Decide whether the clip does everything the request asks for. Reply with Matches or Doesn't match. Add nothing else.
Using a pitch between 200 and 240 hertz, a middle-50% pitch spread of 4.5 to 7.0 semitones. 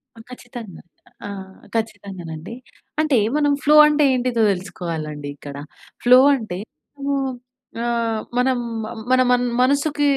Matches